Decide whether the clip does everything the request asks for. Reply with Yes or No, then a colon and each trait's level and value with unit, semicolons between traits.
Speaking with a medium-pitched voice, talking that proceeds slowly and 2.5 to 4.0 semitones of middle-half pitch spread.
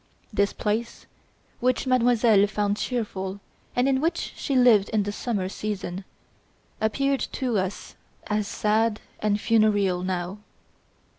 No: high, 210 Hz; slow, 125 wpm; average, 3.1 semitones